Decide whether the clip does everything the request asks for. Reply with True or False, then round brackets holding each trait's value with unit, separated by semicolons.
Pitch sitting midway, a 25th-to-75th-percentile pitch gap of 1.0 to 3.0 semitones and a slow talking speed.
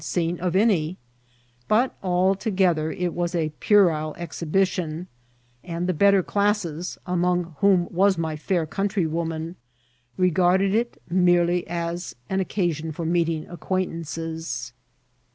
True (175 Hz; 2.5 semitones; 120 wpm)